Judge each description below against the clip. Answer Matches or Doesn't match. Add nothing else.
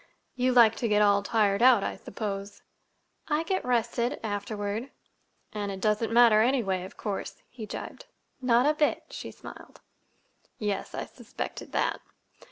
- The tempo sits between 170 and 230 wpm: Doesn't match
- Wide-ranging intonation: Doesn't match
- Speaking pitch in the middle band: Doesn't match